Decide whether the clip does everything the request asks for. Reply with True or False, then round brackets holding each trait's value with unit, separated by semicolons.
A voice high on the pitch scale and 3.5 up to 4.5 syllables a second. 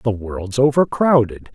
False (120 Hz; 4.0 syllables/s)